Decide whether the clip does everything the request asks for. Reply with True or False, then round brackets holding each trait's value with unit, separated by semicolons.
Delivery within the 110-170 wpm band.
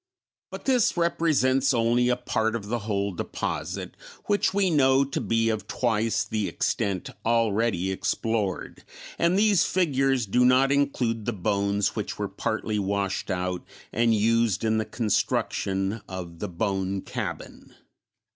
True (140 wpm)